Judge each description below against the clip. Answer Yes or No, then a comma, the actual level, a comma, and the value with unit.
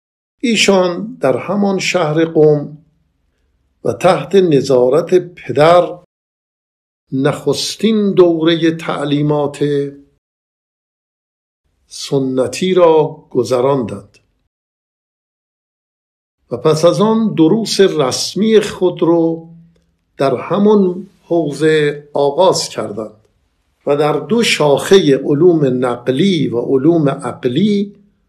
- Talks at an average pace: No, slow, 80 wpm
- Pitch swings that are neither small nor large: No, wide, 6.1 semitones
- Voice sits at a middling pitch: Yes, medium, 150 Hz